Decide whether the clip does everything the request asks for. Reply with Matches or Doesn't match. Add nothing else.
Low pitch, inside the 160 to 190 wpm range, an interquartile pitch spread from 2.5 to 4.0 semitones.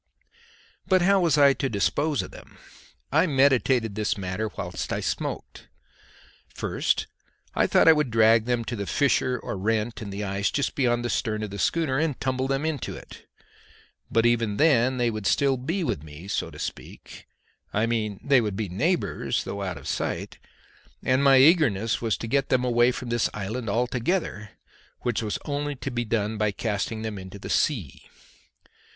Doesn't match